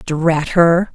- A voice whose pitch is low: No, medium, 165 Hz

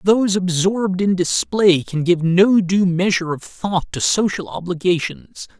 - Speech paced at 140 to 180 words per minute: Yes, average, 150 wpm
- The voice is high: No, medium, 175 Hz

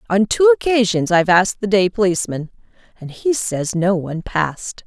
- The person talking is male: No, female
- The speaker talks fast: No, average, 175 wpm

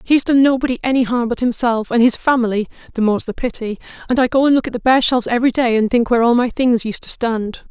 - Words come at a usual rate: No, fast, 250 wpm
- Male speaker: No, female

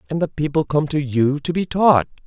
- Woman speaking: No, male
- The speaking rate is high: Yes, fast, 240 wpm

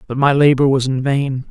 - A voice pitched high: No, low, 135 Hz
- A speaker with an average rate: No, fast, 240 wpm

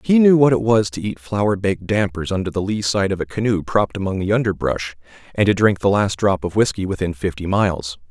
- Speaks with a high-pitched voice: No, low, 100 Hz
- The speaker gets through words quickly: Yes, fast, 235 wpm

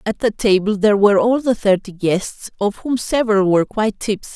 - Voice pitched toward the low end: No, high, 210 Hz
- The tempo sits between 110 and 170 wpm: No, fast, 205 wpm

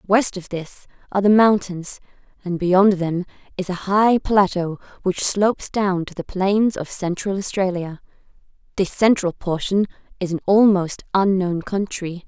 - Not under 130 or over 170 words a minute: Yes, average, 145 wpm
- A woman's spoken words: Yes, female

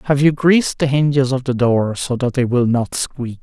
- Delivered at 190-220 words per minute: No, fast, 245 wpm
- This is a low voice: Yes, low, 130 Hz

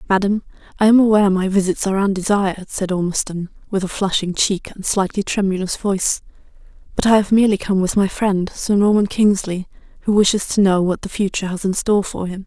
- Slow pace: No, average, 195 wpm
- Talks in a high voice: Yes, high, 195 Hz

